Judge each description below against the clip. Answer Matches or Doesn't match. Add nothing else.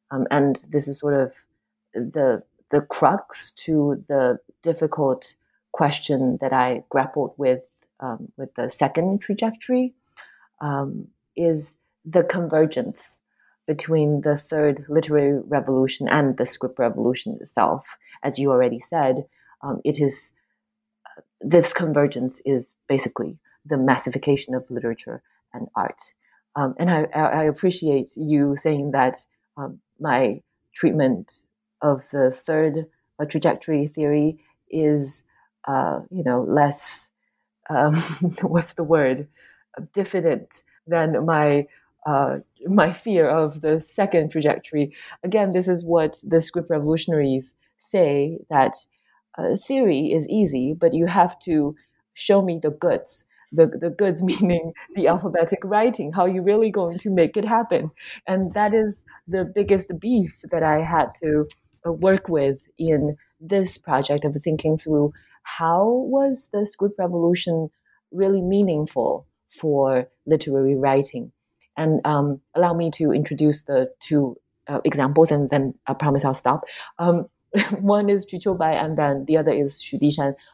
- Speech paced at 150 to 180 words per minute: Doesn't match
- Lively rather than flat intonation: Doesn't match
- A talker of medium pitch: Matches